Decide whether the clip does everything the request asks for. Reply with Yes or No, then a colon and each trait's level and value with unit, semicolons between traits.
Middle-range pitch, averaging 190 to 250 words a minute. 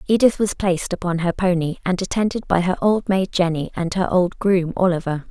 Yes: medium, 180 Hz; fast, 205 wpm